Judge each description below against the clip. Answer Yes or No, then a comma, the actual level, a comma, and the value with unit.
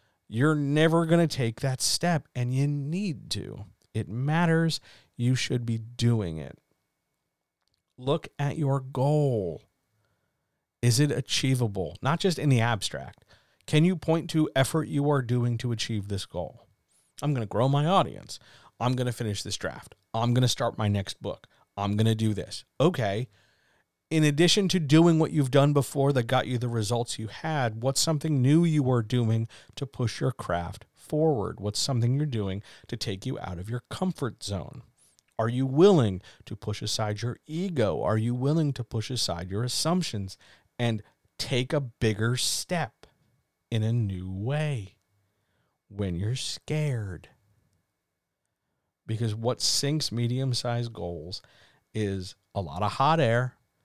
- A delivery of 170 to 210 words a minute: No, average, 160 wpm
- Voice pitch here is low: Yes, low, 120 Hz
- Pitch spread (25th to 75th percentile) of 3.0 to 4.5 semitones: No, average, 5.2 semitones